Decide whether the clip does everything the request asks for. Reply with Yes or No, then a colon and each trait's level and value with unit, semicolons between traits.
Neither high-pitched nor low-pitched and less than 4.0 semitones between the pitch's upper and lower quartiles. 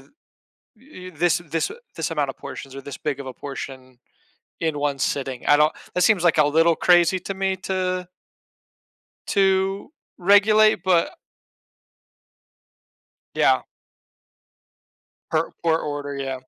No: medium, 165 Hz; average, 4.8 semitones